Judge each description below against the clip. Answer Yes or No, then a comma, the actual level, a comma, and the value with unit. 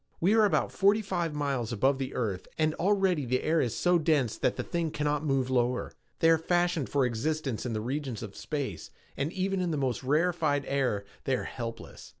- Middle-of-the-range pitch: Yes, medium, 145 Hz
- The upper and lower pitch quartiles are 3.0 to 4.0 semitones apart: No, average, 4.7 semitones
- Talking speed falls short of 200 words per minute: No, fast, 205 wpm